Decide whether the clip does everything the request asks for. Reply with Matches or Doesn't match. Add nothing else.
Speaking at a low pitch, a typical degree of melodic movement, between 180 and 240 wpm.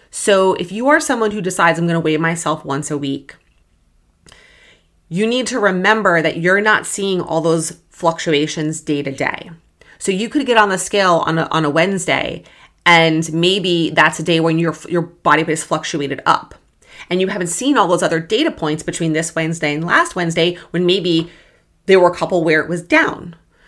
Doesn't match